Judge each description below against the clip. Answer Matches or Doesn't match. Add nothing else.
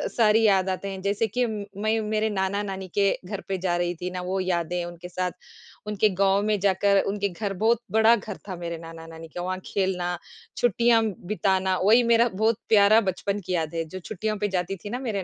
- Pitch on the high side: Matches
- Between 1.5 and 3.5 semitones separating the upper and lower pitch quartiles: Matches